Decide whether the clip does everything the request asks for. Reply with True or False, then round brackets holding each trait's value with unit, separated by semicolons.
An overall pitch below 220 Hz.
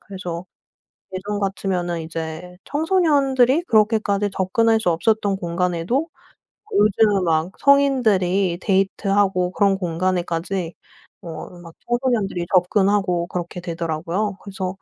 True (190 Hz)